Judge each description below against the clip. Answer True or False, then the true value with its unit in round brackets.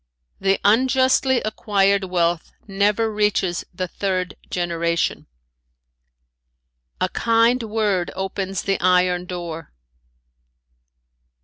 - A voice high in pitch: True (195 Hz)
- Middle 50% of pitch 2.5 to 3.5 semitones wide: True (3.1 semitones)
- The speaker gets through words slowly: True (85 wpm)